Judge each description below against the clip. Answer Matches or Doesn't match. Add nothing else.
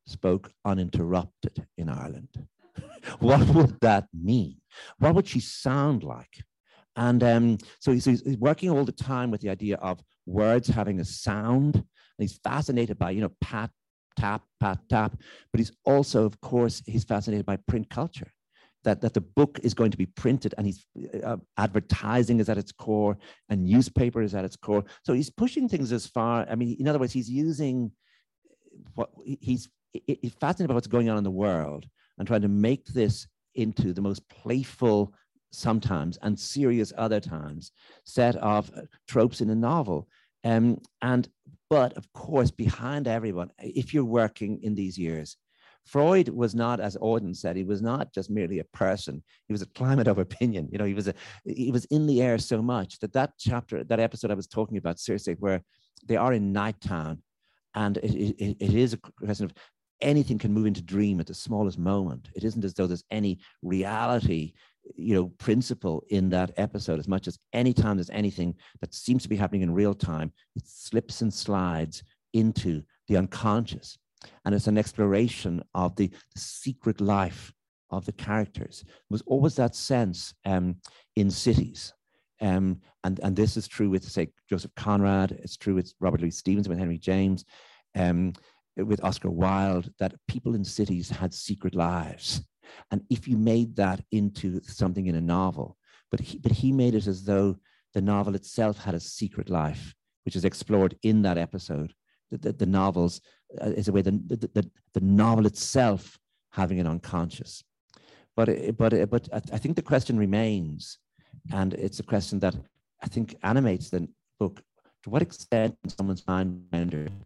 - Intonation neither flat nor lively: Matches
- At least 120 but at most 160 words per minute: Doesn't match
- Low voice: Matches